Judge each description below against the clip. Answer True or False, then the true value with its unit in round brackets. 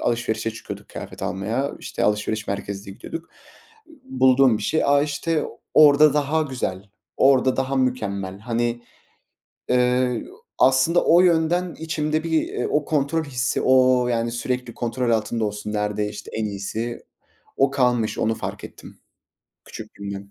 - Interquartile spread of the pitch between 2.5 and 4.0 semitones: False (4.7 semitones)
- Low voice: True (125 Hz)